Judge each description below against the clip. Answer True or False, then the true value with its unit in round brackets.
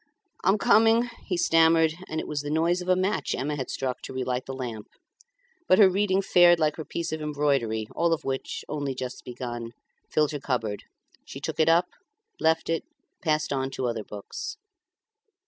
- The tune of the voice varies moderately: True (4.8 semitones)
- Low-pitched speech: False (150 Hz)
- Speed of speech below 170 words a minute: False (185 wpm)